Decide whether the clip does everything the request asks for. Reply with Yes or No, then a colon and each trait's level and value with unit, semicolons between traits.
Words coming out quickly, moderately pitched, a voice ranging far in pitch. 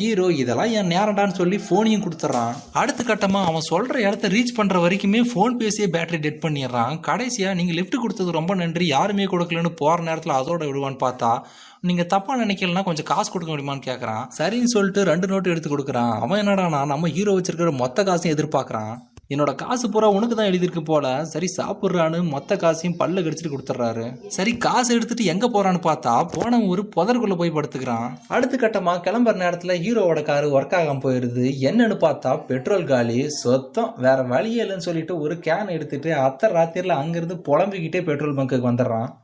Yes: fast, 165 wpm; medium, 170 Hz; wide, 5.8 semitones